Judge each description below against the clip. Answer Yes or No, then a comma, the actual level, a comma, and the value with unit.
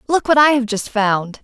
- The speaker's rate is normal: No, fast, 250 wpm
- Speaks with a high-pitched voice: Yes, high, 245 Hz